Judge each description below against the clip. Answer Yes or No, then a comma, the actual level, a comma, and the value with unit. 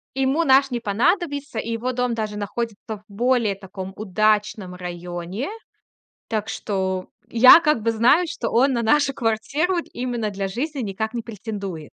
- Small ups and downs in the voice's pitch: No, average, 4.5 semitones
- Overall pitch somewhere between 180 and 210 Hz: No, high, 225 Hz